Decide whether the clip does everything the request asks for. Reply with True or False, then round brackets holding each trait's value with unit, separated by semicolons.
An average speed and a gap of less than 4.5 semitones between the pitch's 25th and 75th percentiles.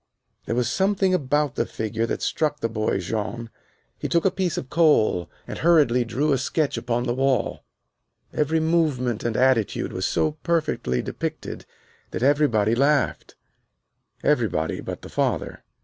False (150 wpm; 5.2 semitones)